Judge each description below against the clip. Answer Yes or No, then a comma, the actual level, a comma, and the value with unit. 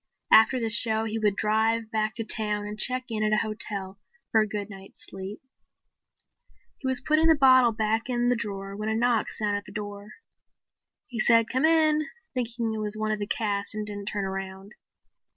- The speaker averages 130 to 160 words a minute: No, average, 200 wpm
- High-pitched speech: Yes, high, 215 Hz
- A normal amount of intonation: No, narrow, 2.1 semitones